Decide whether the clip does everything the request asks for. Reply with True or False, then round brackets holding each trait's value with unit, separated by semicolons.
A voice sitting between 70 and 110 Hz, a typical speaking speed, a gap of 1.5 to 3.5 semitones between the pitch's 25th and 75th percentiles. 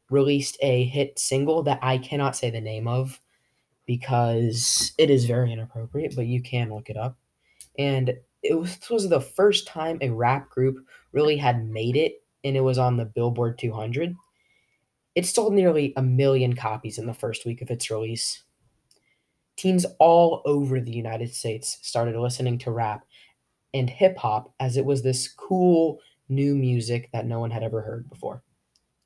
False (130 Hz; 170 wpm; 3.2 semitones)